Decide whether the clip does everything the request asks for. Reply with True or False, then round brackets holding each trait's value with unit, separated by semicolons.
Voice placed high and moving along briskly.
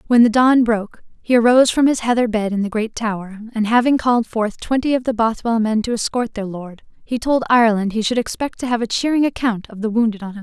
True (230 Hz; 255 wpm)